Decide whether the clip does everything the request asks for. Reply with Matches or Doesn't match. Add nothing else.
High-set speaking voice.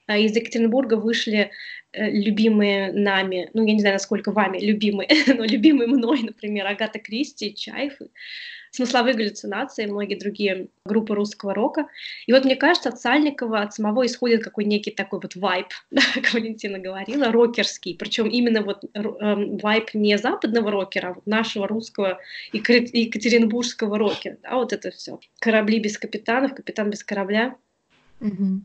Matches